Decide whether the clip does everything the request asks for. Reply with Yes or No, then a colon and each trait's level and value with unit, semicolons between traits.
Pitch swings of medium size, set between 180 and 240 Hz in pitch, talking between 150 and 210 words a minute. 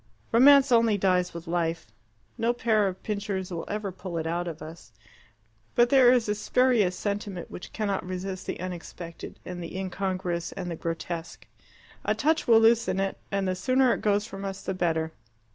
Yes: average, 4.0 semitones; high, 190 Hz; average, 180 wpm